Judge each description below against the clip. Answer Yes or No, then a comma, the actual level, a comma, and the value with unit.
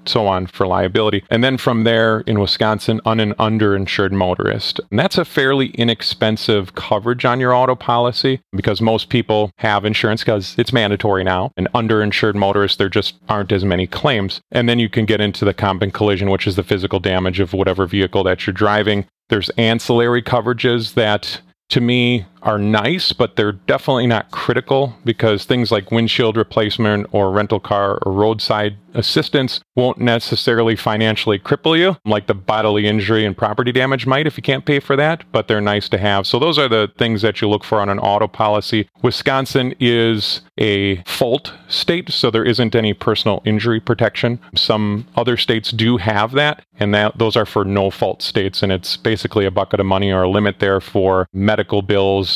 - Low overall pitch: Yes, low, 110 Hz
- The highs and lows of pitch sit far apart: No, average, 2.9 semitones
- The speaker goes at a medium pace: Yes, average, 190 wpm